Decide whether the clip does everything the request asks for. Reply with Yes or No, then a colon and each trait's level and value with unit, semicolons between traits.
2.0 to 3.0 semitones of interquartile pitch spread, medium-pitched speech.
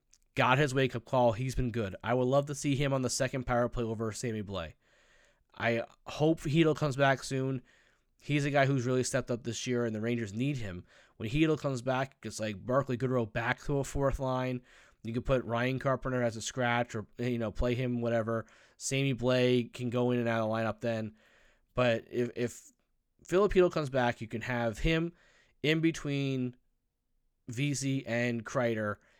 No: narrow, 2.6 semitones; low, 125 Hz